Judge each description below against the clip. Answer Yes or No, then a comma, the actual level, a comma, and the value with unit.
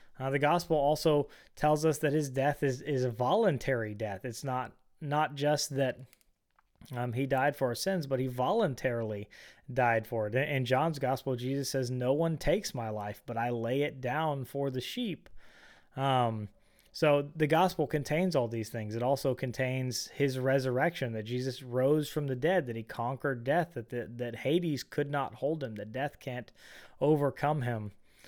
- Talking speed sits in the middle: Yes, average, 180 wpm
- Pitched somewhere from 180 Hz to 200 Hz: No, low, 130 Hz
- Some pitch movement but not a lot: Yes, average, 3.2 semitones